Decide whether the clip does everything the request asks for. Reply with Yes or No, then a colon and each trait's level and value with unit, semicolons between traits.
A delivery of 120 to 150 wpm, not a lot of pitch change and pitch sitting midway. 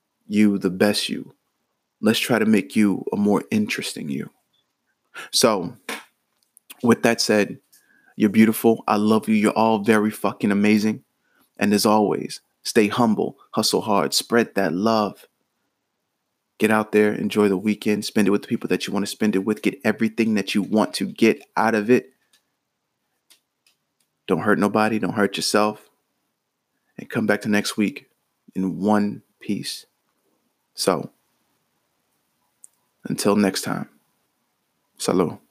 No: average, 145 wpm; narrow, 0.9 semitones; low, 105 Hz